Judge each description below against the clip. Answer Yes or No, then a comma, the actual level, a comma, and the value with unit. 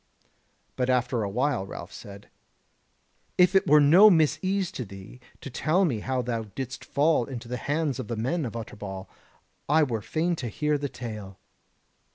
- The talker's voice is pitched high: No, low, 130 Hz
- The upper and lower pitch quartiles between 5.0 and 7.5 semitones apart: Yes, wide, 5.4 semitones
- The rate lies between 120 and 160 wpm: No, average, 175 wpm